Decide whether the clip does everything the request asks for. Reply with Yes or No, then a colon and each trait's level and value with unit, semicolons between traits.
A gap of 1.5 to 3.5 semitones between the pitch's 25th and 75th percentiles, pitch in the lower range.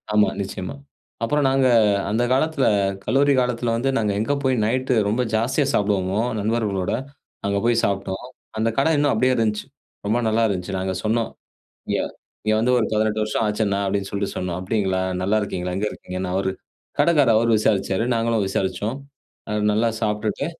Yes: average, 3.1 semitones; low, 110 Hz